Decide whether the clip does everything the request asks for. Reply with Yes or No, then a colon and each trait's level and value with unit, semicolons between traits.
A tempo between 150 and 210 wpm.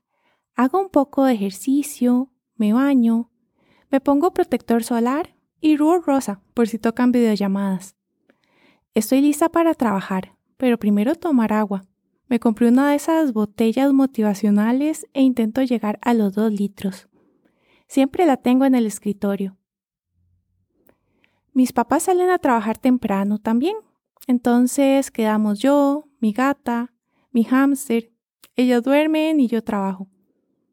No: slow, 125 wpm